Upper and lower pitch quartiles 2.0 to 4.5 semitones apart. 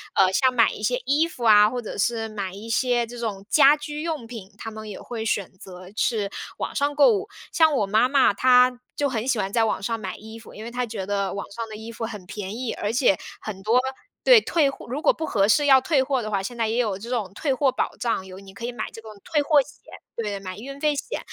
Yes: average, 4.2 semitones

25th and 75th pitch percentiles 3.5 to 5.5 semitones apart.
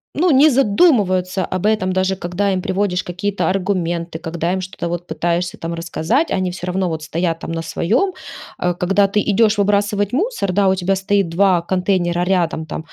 No: average, 2.7 semitones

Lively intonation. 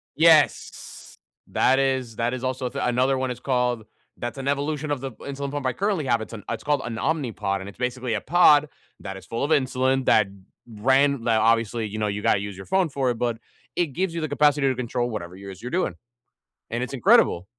No: average, 3.7 semitones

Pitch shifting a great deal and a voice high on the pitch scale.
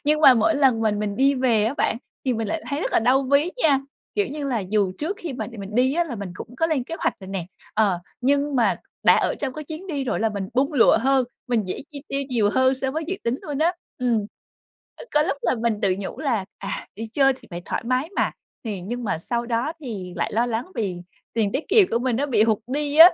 No: average, 4.7 semitones; very high, 255 Hz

